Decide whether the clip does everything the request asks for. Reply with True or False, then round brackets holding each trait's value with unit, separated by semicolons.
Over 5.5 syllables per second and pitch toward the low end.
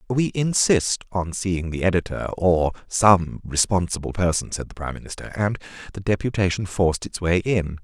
False (5.0 syllables/s; 95 Hz)